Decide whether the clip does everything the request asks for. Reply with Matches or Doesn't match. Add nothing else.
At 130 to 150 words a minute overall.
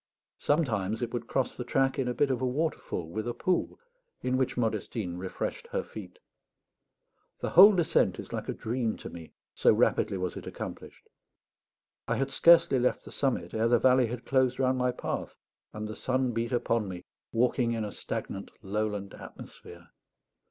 Doesn't match